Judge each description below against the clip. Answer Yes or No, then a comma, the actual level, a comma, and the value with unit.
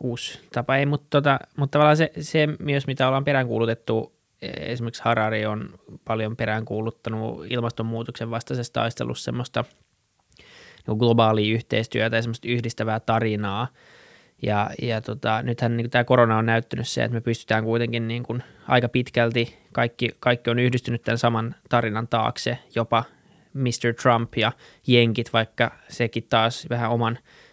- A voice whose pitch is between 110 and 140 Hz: Yes, low, 115 Hz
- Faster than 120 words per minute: Yes, average, 140 wpm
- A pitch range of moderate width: No, narrow, 1.6 semitones